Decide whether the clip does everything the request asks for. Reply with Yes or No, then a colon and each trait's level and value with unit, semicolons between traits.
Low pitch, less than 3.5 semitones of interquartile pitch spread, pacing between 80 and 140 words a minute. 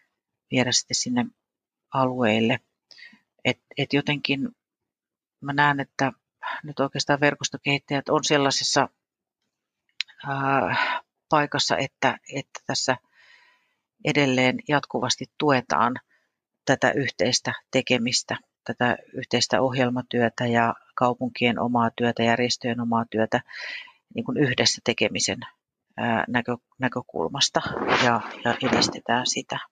Yes: low, 130 Hz; average, 2.9 semitones; slow, 95 wpm